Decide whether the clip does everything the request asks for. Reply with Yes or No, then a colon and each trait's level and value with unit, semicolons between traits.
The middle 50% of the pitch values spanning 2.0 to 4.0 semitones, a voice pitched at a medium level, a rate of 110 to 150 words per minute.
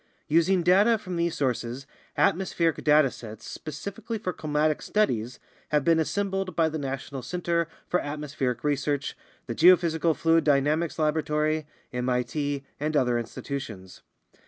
Yes: average, 3.7 semitones; medium, 155 Hz; slow, 135 wpm